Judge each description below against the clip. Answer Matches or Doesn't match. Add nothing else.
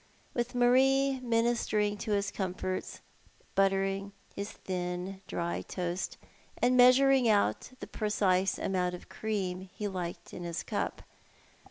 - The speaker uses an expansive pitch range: Doesn't match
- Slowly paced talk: Matches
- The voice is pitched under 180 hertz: Doesn't match